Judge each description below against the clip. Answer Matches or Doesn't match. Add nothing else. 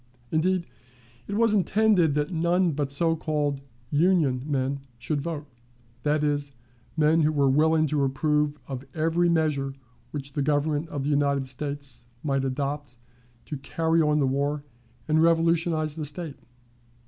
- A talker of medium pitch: Matches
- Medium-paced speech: Matches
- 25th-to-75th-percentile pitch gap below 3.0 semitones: Matches